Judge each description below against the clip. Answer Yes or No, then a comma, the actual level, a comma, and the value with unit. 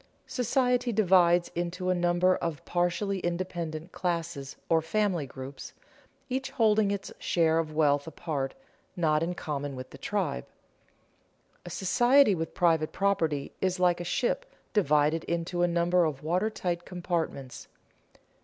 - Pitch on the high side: No, medium, 175 Hz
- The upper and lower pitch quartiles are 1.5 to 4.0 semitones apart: Yes, average, 3.2 semitones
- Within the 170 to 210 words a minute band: No, slow, 135 wpm